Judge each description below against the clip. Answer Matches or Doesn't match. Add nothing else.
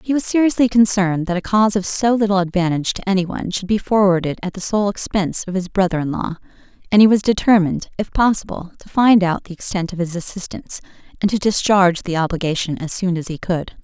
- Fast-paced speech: Matches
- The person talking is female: Matches